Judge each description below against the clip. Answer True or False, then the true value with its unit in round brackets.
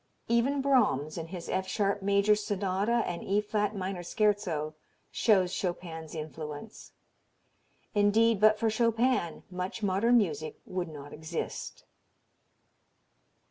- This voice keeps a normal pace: False (115 wpm)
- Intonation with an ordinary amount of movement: True (4.0 semitones)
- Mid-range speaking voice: False (195 Hz)